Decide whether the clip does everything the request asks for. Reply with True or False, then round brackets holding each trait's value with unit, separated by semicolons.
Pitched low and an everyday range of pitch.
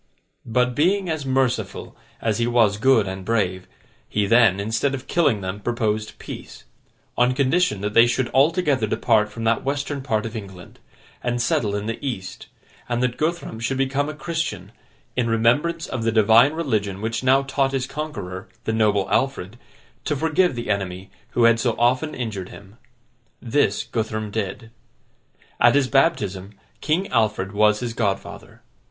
True (115 Hz; 4.2 semitones)